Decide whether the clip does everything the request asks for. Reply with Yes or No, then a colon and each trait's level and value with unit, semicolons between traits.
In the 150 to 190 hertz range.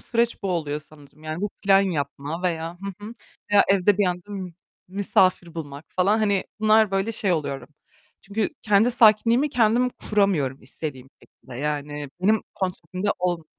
Yes: medium, 185 Hz